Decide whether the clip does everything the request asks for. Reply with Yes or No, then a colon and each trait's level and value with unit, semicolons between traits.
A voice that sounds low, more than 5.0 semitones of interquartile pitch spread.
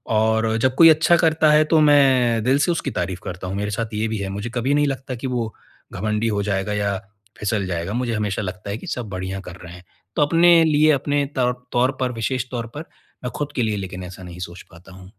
Yes: low, 110 Hz; wide, 5.4 semitones